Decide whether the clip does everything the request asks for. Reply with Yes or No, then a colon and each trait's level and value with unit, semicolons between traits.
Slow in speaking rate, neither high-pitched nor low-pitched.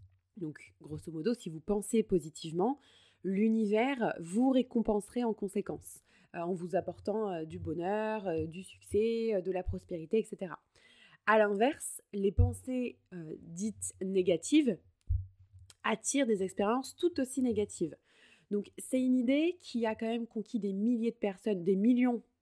No: slow, 135 wpm; high, 205 Hz